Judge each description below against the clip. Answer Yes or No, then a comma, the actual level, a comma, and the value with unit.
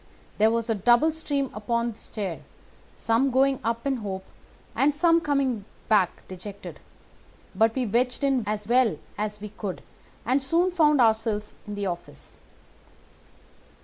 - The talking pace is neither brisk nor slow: Yes, average, 150 wpm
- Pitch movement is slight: No, average, 4.5 semitones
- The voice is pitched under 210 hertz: No, high, 230 Hz